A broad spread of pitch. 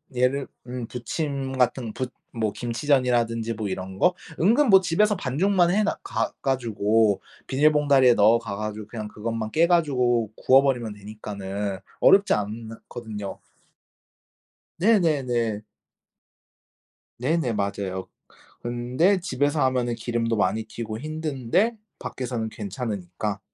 No: average, 4.9 semitones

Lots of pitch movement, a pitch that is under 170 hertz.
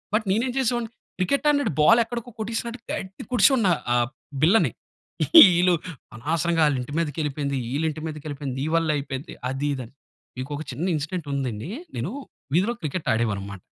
Yes: wide, 7.2 semitones; medium, 155 Hz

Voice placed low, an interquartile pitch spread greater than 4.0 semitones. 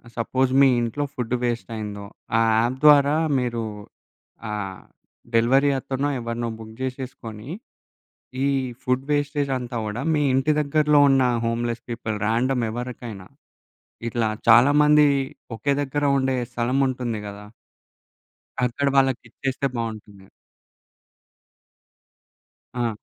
No: low, 125 Hz; average, 2.9 semitones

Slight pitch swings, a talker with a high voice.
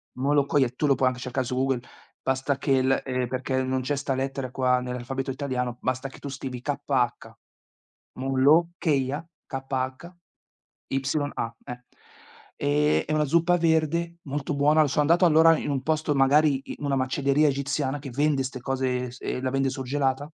No: narrow, 2.2 semitones; low, 135 Hz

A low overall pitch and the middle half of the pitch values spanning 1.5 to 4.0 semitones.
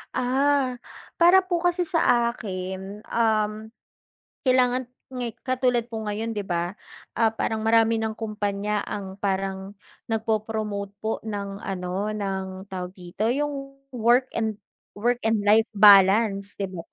No: high, 215 Hz; average, 3.3 semitones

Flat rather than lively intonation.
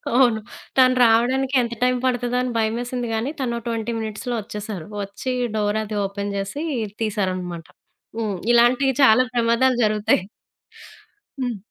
No: average, 3.0 semitones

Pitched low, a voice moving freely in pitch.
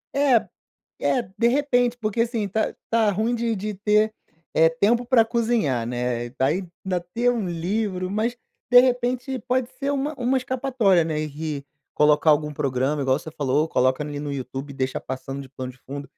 No: high, 190 Hz; wide, 8.8 semitones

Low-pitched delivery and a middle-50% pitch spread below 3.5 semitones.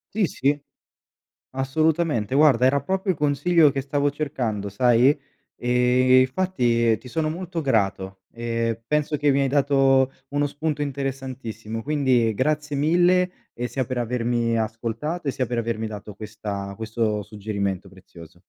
No: low, 130 Hz; average, 4.5 semitones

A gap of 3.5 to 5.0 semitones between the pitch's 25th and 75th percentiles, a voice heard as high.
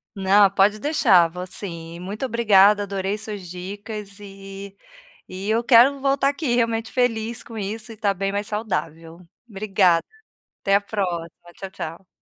No: average, 2.7 semitones; high, 200 Hz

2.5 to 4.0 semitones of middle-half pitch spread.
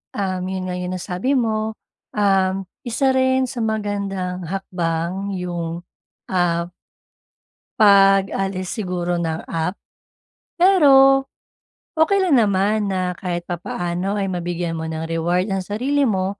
Yes: average, 3.5 semitones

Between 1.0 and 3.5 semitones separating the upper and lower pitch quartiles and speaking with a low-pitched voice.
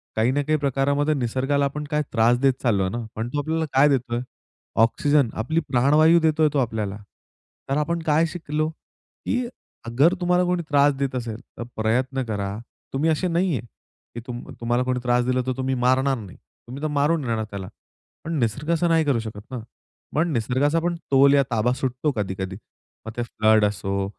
No: average, 4.4 semitones; low, 130 Hz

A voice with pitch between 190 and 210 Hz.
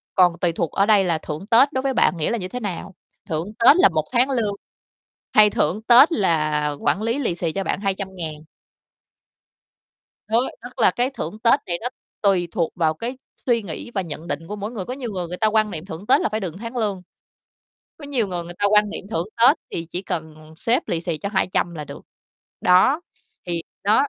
Yes: high, 195 Hz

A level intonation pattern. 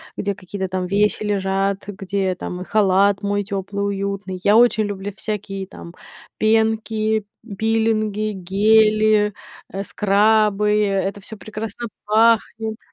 Yes: narrow, 1.8 semitones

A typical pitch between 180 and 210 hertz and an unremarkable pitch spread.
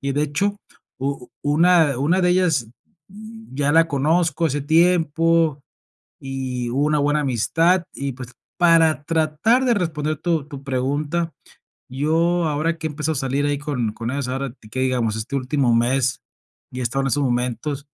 No: medium, 145 Hz; average, 3.7 semitones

